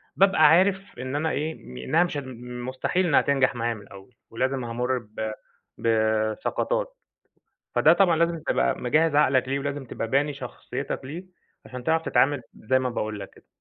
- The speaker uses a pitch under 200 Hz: Yes, low, 135 Hz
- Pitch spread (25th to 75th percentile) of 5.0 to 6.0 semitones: Yes, average, 5.3 semitones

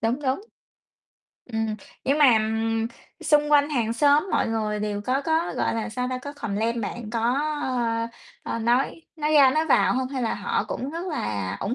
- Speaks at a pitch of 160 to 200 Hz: No, very high, 250 Hz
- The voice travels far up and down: No, average, 4.6 semitones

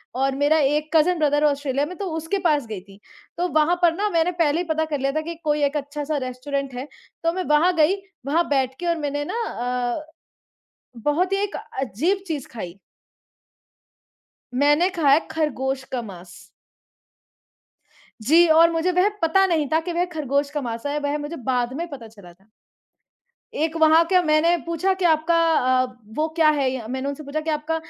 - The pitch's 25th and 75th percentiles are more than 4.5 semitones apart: No, average, 3.3 semitones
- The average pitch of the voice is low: No, very high, 300 Hz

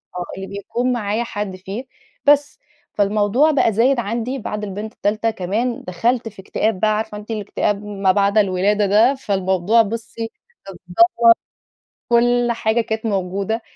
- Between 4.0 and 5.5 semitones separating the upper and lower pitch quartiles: No, average, 2.9 semitones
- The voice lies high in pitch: Yes, high, 215 Hz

